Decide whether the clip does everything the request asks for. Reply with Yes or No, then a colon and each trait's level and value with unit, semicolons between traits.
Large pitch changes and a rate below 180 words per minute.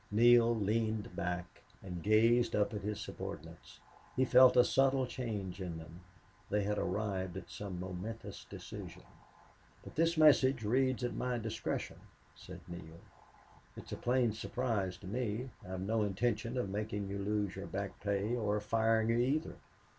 No: average, 3.6 semitones; average, 160 wpm